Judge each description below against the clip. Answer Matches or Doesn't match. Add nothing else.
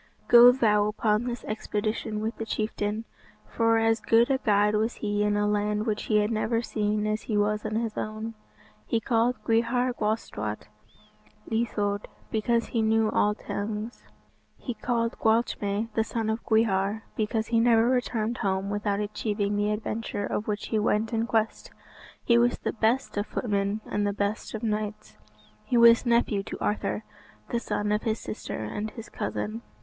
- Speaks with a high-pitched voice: Matches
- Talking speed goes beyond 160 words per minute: Matches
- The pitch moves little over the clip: Matches